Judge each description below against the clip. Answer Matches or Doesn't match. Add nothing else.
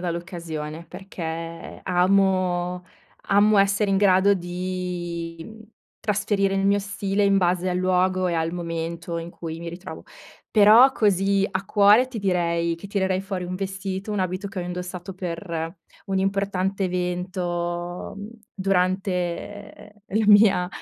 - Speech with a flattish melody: Matches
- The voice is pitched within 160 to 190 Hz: Matches